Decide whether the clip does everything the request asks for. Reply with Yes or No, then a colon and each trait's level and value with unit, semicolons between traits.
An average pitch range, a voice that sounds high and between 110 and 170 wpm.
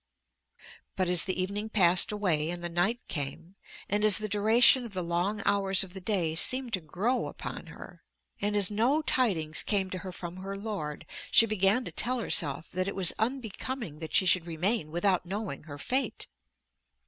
No: average, 3.7 semitones; high, 195 Hz; average, 185 wpm